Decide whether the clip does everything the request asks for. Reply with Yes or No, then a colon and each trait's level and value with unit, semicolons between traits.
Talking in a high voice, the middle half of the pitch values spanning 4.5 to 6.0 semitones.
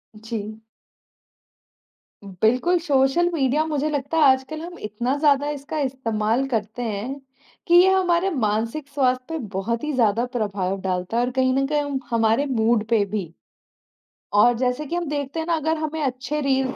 Yes: very high, 260 Hz; average, 5.1 semitones